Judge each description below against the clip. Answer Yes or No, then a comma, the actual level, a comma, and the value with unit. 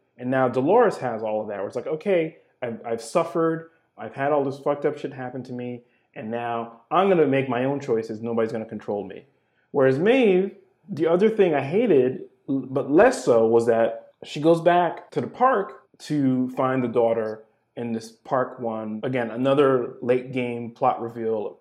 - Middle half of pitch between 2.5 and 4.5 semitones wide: No, average, 5.3 semitones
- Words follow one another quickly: No, average, 190 wpm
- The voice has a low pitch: Yes, low, 130 Hz